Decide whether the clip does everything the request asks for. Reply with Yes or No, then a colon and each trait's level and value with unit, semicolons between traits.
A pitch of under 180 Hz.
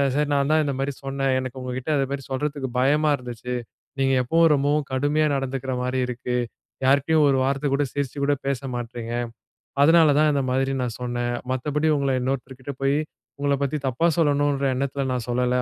Yes: low, 135 Hz